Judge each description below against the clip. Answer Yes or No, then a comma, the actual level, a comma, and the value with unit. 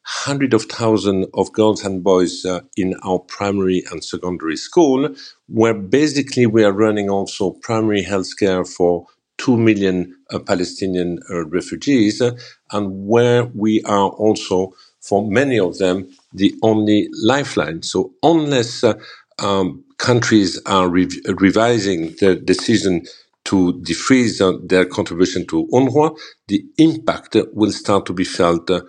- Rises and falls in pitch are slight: No, average, 3.4 semitones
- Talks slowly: No, average, 145 wpm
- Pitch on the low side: Yes, low, 100 Hz